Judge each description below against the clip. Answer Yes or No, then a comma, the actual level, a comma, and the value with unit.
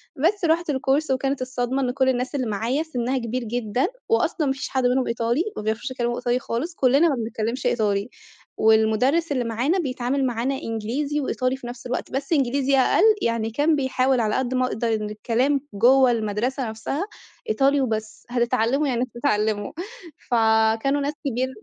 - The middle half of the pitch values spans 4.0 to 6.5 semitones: No, average, 3.0 semitones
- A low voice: No, very high, 255 Hz